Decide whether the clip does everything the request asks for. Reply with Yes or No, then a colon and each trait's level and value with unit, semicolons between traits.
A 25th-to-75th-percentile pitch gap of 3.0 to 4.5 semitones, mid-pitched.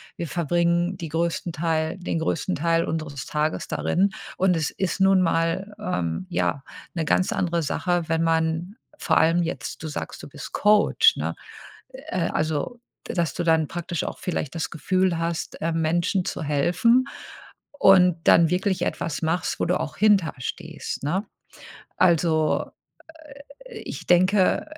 No: narrow, 2.4 semitones; medium, 170 Hz